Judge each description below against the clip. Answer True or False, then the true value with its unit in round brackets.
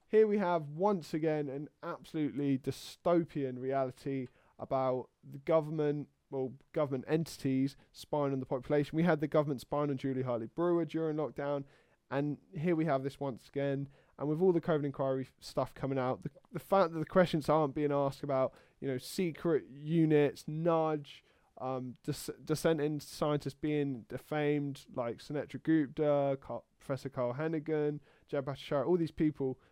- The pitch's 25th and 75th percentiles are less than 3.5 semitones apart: True (2.7 semitones)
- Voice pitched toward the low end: False (145 Hz)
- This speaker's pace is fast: False (155 wpm)